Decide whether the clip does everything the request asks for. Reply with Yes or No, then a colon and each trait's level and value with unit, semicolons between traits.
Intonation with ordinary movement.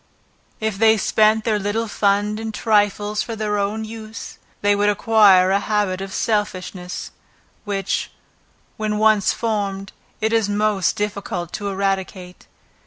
No: narrow, 1.7 semitones